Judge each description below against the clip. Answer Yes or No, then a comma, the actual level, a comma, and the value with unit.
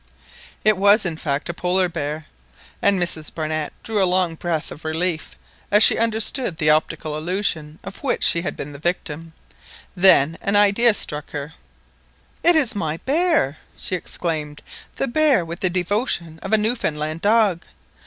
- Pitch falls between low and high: Yes, medium, 175 Hz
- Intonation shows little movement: No, average, 4.8 semitones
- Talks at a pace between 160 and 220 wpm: Yes, average, 165 wpm